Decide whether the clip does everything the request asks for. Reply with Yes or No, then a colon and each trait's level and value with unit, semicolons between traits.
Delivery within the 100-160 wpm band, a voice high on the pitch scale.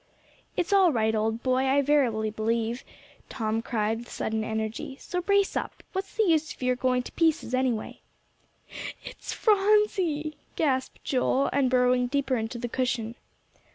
Yes: average, 155 wpm; very high, 255 Hz